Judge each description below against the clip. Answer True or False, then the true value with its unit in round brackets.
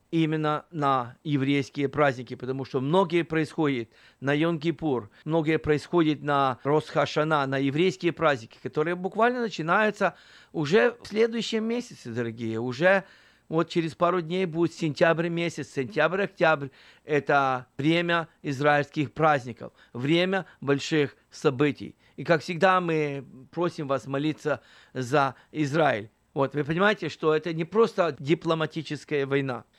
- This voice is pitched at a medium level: True (155 Hz)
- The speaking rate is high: False (120 wpm)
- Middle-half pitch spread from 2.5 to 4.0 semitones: True (3.5 semitones)